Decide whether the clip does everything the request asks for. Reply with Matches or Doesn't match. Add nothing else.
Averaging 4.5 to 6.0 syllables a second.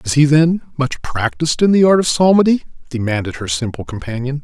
Matches